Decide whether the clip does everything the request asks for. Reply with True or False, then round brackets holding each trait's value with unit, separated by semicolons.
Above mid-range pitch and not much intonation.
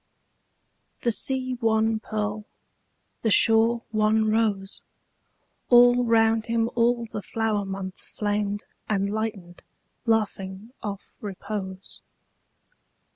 True (220 Hz; 2.1 semitones)